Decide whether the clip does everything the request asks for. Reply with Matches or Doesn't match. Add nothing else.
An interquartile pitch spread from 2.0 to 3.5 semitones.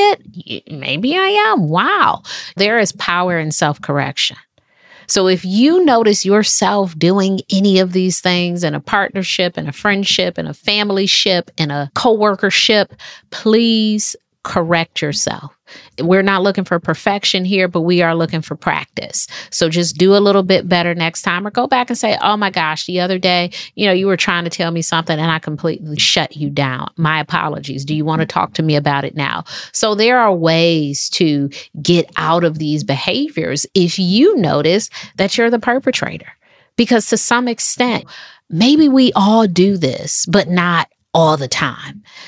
Doesn't match